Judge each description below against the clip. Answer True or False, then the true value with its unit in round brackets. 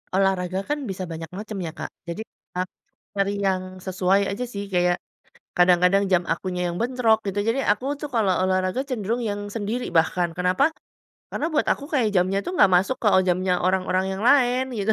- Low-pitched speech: False (195 Hz)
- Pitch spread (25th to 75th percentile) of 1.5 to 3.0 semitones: False (3.9 semitones)